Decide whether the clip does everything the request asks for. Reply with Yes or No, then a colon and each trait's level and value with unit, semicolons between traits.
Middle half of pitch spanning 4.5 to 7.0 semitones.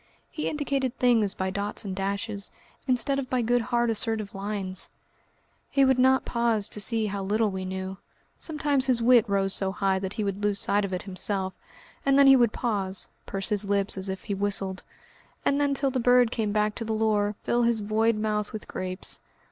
No: average, 3.6 semitones